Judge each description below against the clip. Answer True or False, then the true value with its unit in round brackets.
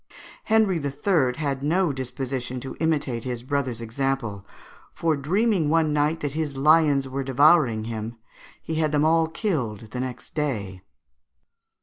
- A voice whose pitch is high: False (140 Hz)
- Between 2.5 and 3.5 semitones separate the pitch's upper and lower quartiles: False (4.1 semitones)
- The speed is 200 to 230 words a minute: False (140 wpm)